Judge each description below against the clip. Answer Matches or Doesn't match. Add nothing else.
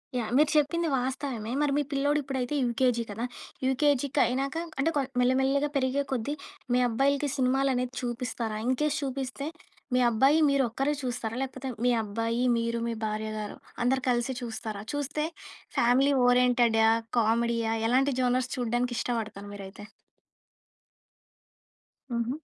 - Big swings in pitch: Doesn't match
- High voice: Matches